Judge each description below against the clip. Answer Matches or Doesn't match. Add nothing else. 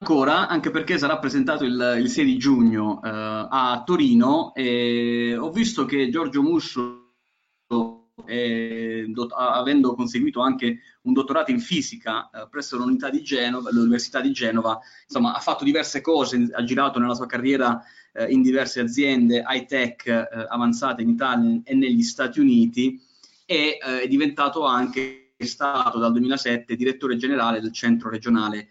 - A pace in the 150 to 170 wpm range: Matches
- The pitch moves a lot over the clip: Doesn't match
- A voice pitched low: Matches